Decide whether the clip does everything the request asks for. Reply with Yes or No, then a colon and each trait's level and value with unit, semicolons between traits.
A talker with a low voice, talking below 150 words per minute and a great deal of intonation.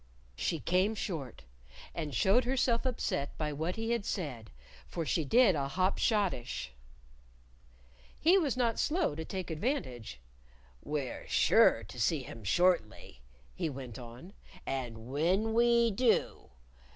No: medium, 175 Hz; slow, 135 wpm; wide, 8.9 semitones